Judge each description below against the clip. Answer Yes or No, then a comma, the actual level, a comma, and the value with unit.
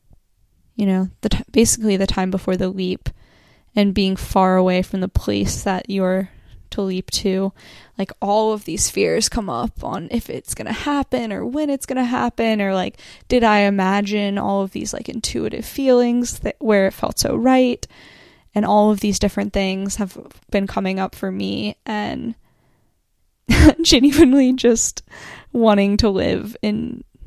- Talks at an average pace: Yes, average, 170 wpm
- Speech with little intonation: No, average, 3.3 semitones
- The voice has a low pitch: No, high, 200 Hz